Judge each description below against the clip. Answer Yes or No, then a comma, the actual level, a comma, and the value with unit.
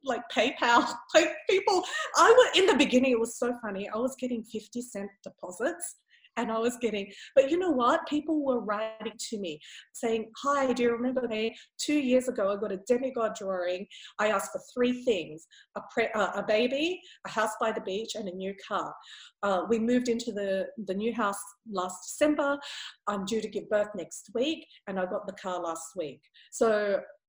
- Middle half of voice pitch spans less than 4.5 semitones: No, average, 5.3 semitones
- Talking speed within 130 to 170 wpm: No, average, 200 wpm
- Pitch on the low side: No, high, 230 Hz